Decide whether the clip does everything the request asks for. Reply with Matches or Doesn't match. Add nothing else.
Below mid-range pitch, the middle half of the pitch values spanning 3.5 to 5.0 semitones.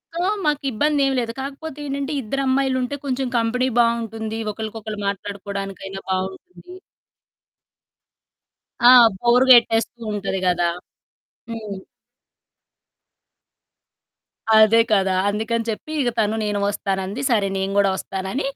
Doesn't match